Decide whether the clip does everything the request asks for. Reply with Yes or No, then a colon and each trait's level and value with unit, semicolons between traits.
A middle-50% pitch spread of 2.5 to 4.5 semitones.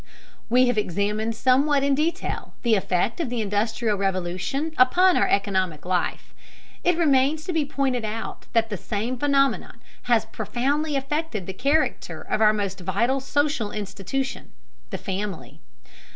No: wide, 5.4 semitones